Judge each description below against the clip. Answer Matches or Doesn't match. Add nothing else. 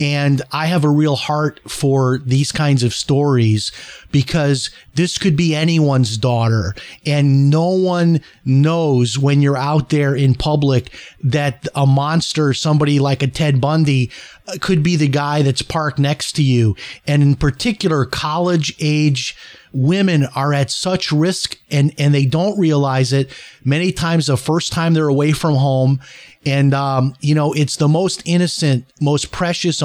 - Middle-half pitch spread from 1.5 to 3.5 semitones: Matches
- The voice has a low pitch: Doesn't match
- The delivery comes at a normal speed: Matches